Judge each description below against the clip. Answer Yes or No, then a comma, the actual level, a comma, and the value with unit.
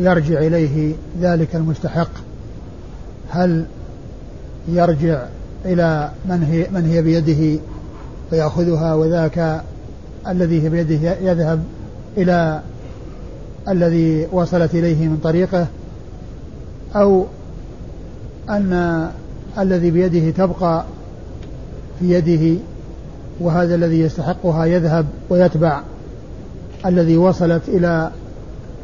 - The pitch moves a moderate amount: No, narrow, 1.7 semitones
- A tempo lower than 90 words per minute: Yes, average, 75 wpm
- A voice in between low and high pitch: Yes, medium, 165 Hz